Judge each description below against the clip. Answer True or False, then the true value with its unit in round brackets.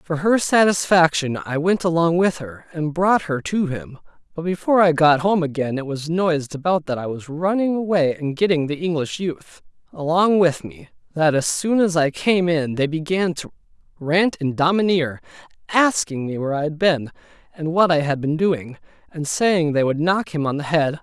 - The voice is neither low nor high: True (165 Hz)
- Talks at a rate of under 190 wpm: False (200 wpm)